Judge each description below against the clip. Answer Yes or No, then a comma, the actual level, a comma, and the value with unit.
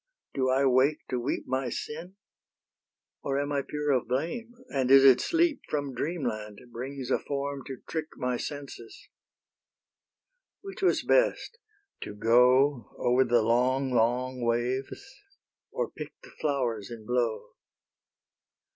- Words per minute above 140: No, slow, 135 wpm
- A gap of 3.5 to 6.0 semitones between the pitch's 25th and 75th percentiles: No, average, 2.7 semitones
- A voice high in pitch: No, low, 130 Hz